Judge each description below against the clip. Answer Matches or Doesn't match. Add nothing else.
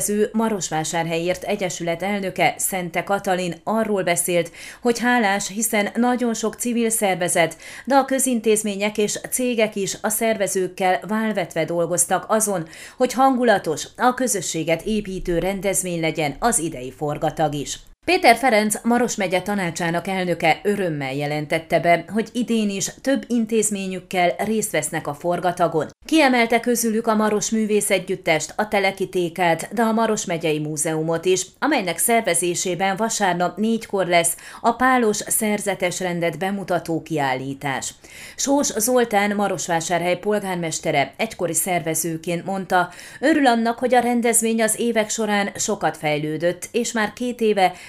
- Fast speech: Doesn't match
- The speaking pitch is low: Doesn't match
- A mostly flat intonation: Doesn't match